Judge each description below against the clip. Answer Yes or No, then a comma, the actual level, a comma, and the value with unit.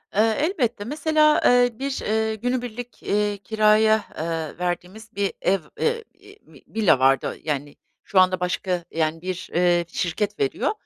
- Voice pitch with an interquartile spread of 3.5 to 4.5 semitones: No, average, 5.3 semitones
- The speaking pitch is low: No, high, 210 Hz